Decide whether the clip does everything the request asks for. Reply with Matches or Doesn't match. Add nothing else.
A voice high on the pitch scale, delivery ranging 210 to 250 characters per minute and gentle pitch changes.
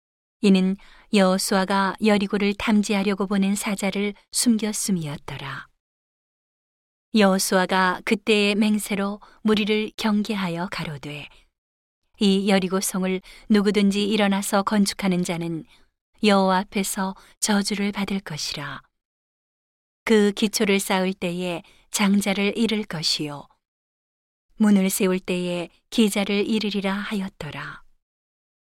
Matches